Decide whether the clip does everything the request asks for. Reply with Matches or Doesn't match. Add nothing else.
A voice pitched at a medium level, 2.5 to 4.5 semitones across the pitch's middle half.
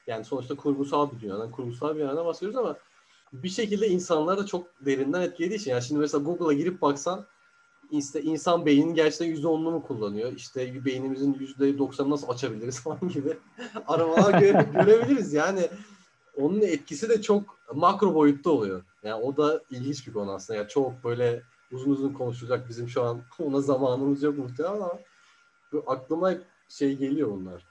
Doesn't match